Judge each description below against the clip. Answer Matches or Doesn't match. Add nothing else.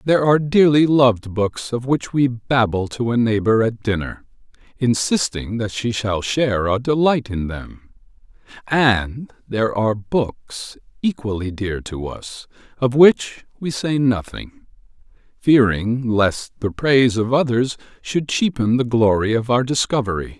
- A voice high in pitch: Doesn't match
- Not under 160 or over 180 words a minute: Doesn't match